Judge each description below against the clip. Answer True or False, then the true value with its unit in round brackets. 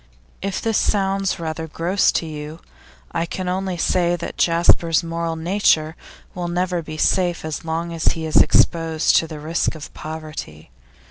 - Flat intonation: True (2.1 semitones)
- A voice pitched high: False (165 Hz)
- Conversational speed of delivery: True (160 wpm)